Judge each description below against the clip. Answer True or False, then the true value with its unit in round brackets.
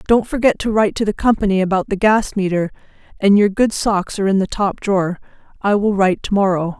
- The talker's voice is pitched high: True (200 Hz)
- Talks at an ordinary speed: False (220 wpm)